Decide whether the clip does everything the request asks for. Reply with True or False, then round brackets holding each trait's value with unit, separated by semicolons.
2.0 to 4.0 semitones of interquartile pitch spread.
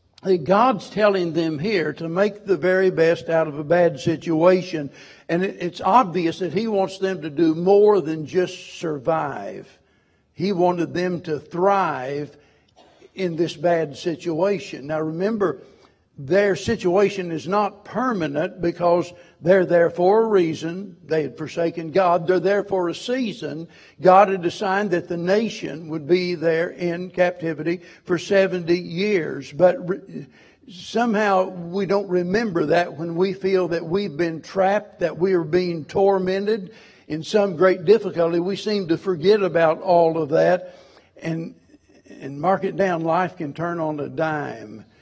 True (2.8 semitones)